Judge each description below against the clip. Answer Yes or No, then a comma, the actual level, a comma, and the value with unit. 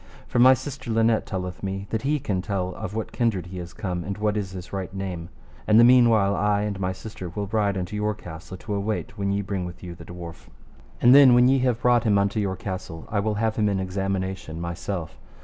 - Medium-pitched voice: No, low, 100 Hz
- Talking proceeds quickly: Yes, fast, 235 wpm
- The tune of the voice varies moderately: Yes, average, 3.0 semitones